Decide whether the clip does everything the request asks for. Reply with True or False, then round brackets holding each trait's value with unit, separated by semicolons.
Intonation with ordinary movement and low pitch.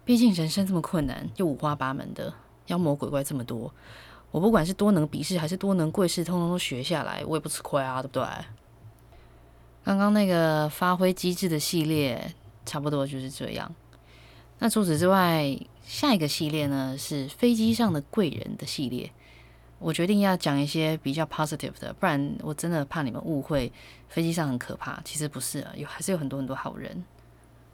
False (4.9 semitones; 155 Hz)